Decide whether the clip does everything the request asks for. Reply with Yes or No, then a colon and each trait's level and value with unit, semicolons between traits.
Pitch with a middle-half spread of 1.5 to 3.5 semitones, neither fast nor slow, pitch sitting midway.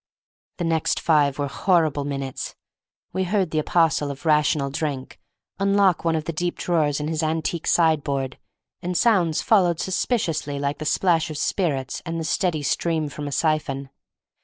Yes: average, 3.1 semitones; average, 160 wpm; medium, 155 Hz